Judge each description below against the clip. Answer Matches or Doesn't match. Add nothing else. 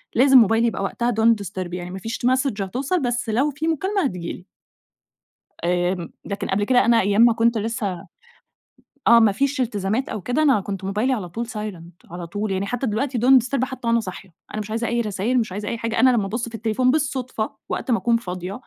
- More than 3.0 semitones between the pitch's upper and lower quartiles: Matches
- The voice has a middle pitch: Doesn't match